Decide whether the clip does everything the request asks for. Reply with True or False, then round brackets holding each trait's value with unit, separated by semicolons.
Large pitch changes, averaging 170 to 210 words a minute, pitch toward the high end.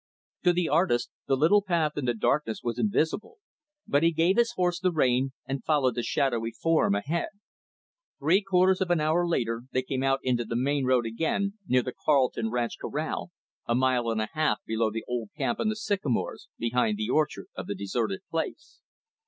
False (6.4 semitones; 195 wpm; 140 Hz)